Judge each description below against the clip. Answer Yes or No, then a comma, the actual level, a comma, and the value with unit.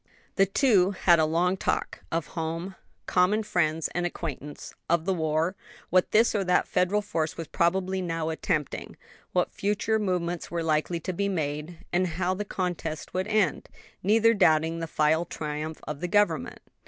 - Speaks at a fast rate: No, average, 165 wpm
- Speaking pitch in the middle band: Yes, medium, 175 Hz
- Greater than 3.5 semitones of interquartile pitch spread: No, average, 3.1 semitones